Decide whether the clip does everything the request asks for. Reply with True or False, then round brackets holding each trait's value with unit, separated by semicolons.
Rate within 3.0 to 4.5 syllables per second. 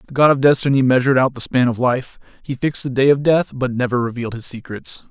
False (6.4 syllables/s)